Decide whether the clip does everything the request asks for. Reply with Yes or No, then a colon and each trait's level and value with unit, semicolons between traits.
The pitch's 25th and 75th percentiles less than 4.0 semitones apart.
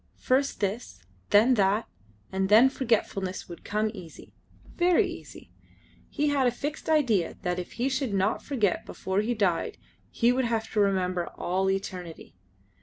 No: average, 4.8 semitones